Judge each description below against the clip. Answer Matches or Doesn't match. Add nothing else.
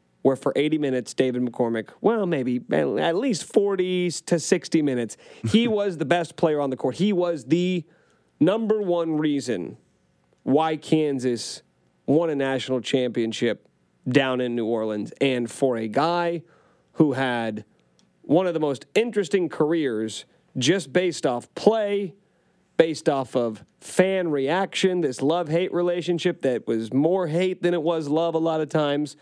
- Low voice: Doesn't match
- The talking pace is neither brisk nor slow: Matches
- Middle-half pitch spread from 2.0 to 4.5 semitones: Doesn't match